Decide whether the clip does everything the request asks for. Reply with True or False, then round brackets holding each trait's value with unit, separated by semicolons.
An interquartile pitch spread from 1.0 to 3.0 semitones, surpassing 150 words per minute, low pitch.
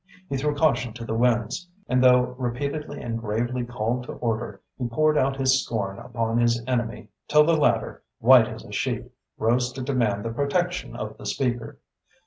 True (2.5 semitones; 180 wpm; 120 Hz)